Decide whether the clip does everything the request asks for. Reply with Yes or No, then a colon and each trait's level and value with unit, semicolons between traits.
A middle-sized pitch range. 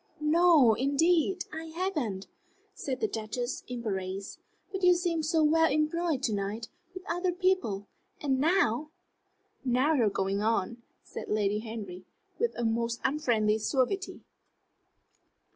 No: wide, 7.2 semitones